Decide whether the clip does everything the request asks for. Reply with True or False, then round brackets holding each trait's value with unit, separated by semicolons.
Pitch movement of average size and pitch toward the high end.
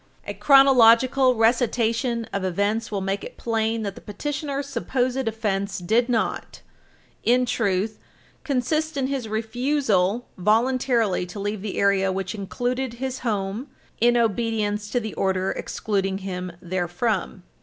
True (4.0 semitones; 225 Hz)